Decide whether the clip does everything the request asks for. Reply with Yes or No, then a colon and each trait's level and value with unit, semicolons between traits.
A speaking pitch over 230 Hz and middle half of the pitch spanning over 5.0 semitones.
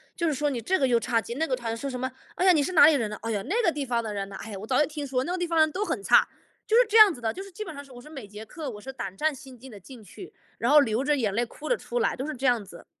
Yes: very high, 265 Hz; wide, 5.5 semitones